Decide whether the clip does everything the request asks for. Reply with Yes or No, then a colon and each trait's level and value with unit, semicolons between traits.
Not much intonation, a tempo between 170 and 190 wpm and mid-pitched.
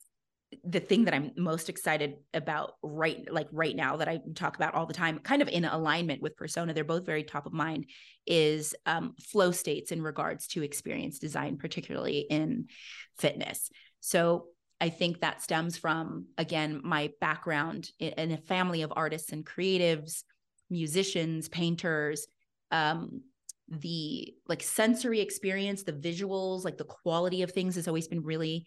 No: narrow, 2.3 semitones; average, 160 wpm; medium, 165 Hz